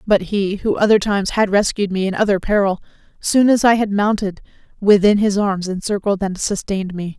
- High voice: Yes, high, 200 Hz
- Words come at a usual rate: Yes, average, 190 wpm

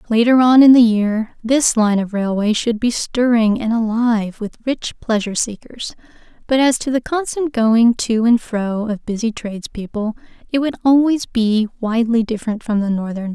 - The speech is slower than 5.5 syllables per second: Yes, 5.0 syllables/s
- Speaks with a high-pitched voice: Yes, high, 230 Hz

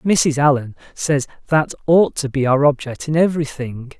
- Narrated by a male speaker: Yes, male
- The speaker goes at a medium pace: Yes, average, 165 wpm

